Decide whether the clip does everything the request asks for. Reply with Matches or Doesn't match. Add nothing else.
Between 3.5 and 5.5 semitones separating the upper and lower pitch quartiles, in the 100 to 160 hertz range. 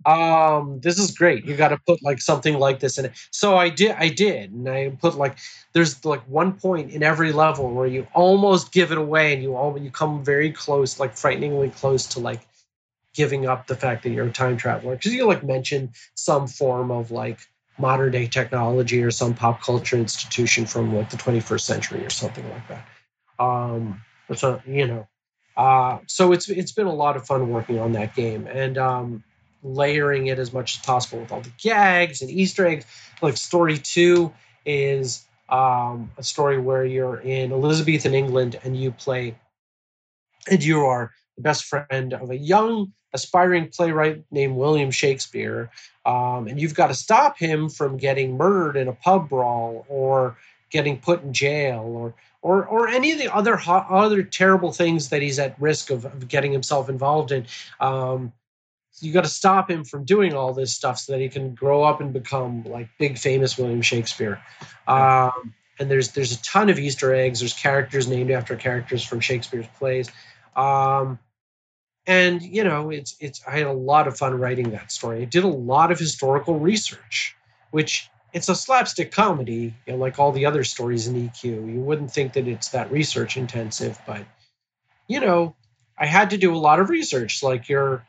Matches